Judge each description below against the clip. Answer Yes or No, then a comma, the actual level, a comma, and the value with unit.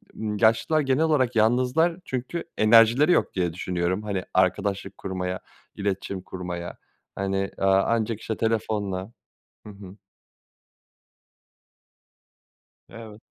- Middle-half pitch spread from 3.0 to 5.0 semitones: Yes, average, 3.5 semitones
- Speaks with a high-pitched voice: No, low, 105 Hz